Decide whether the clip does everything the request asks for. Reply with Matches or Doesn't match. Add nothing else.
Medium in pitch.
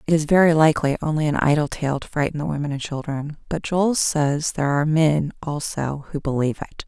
Matches